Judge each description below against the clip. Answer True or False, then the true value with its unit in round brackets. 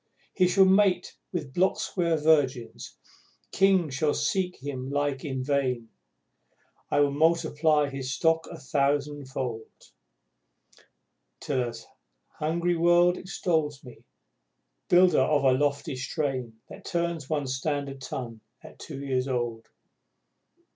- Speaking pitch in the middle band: True (145 Hz)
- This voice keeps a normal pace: False (120 wpm)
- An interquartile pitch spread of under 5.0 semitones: True (4.2 semitones)